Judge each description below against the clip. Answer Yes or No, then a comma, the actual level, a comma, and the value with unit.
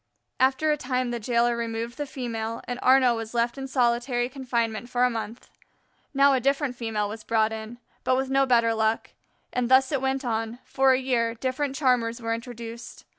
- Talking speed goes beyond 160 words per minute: Yes, average, 190 wpm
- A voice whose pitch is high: Yes, high, 240 Hz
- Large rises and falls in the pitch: No, narrow, 2.4 semitones